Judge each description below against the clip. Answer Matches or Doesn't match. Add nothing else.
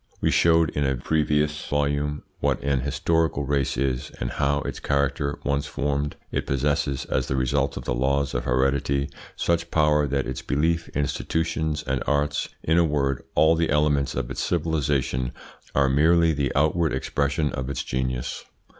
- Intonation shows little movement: Matches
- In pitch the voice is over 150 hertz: Doesn't match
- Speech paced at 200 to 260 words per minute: Doesn't match